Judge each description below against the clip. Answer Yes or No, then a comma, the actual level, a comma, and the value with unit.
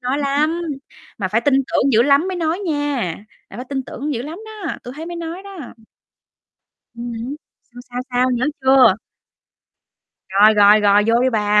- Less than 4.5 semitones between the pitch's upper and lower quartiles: No, average, 5.1 semitones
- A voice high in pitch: Yes, very high, 265 Hz